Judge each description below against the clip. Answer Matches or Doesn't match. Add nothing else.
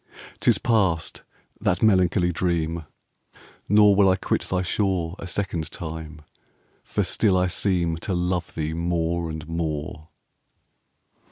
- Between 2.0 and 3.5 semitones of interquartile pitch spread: Matches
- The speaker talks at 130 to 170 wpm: Matches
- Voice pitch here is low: Matches